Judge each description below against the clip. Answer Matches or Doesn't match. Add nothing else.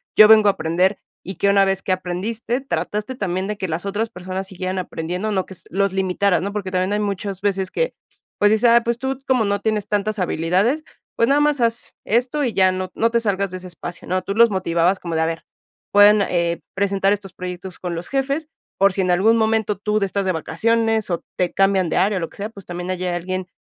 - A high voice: Matches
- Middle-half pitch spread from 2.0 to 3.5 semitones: Matches